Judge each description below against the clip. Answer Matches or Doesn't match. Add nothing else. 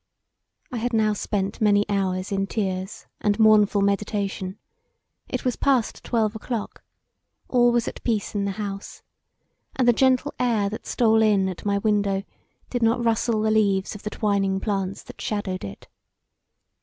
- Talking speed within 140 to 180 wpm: Matches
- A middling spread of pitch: Doesn't match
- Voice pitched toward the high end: Matches